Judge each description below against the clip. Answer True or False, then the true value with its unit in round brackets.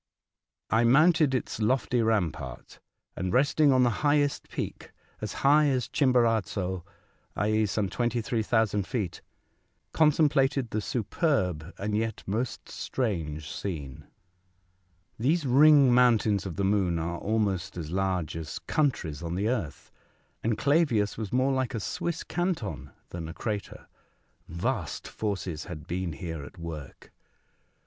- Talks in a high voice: False (110 Hz)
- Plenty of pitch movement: True (6.4 semitones)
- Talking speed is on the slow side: True (130 wpm)